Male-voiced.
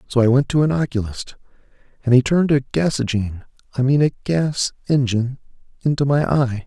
Yes: male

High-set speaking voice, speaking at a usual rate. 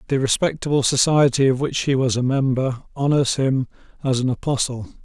No: low, 135 Hz; average, 165 wpm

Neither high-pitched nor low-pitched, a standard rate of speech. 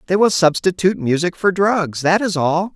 Yes: medium, 180 Hz; average, 195 wpm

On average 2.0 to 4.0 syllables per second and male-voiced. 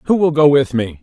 No: 5.8 syllables/s; male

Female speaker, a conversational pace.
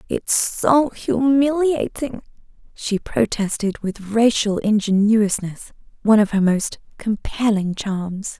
No: female; slow, 95 wpm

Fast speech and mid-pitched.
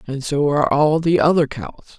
Yes: fast, 210 wpm; medium, 145 Hz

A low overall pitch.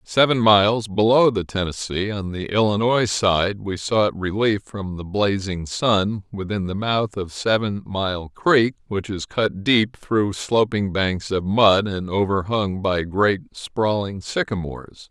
Yes: low, 100 Hz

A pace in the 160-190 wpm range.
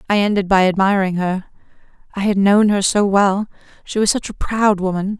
Yes: average, 185 wpm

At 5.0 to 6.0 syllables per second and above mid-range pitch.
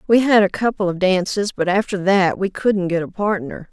Yes: 5.1 syllables/s; high, 195 Hz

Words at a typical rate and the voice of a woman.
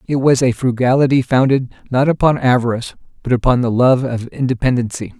No: average, 160 wpm; male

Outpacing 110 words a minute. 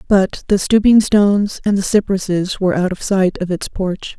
Yes: average, 200 wpm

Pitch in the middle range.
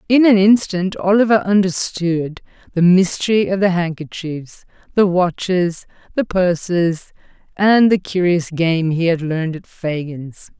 Yes: medium, 180 Hz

